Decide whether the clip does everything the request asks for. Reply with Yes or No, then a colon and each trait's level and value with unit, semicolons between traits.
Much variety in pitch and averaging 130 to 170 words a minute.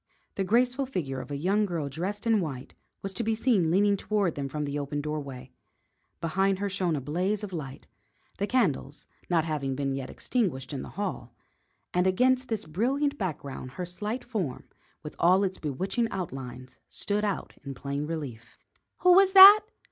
No: wide, 6.8 semitones; average, 180 wpm